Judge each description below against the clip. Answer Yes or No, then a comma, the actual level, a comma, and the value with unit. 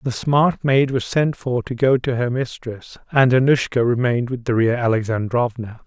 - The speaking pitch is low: Yes, low, 125 Hz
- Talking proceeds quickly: No, average, 175 wpm